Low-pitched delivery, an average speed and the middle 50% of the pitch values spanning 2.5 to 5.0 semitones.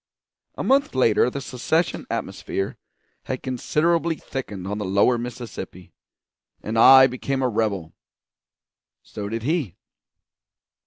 No: low, 125 Hz; slow, 115 wpm; average, 4.5 semitones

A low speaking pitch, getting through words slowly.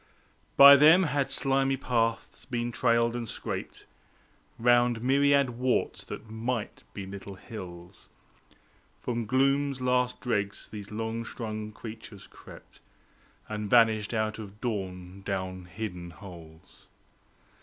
Yes: low, 115 Hz; slow, 115 wpm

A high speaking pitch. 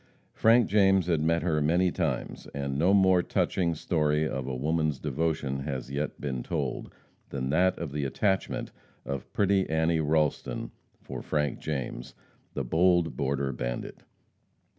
No: very low, 75 Hz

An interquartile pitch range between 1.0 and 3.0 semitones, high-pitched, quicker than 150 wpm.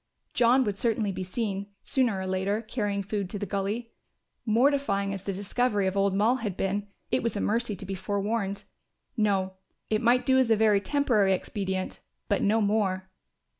Yes: average, 2.7 semitones; high, 205 Hz; average, 180 wpm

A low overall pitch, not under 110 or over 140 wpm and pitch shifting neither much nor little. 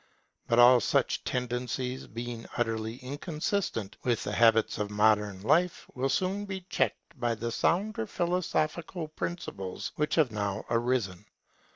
No: low, 125 Hz; slow, 135 wpm; wide, 5.9 semitones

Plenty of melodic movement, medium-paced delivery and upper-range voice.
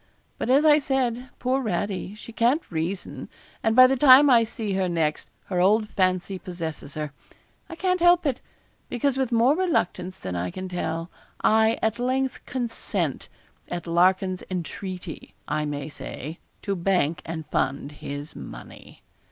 Yes: wide, 7.0 semitones; average, 155 wpm; high, 195 Hz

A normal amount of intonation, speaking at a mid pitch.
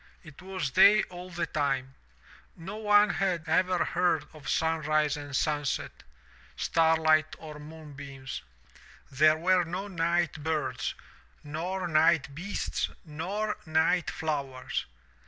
Yes: average, 3.3 semitones; medium, 160 Hz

